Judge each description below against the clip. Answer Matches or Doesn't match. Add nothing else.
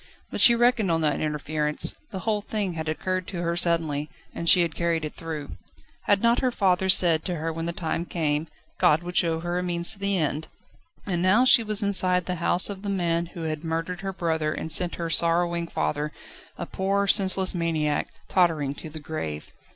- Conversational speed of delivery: Doesn't match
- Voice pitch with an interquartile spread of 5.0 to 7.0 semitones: Doesn't match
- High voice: Doesn't match